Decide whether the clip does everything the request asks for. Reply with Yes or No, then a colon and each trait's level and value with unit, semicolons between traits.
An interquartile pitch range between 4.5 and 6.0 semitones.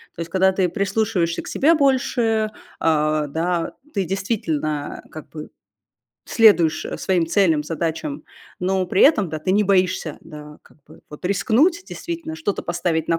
Yes: average, 5.2 semitones